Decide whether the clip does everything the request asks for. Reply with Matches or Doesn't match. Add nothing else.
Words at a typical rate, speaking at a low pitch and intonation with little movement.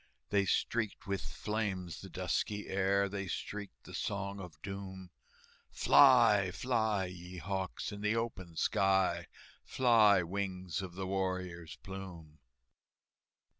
Doesn't match